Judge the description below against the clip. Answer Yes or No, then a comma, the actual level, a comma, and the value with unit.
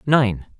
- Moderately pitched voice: No, low, 120 Hz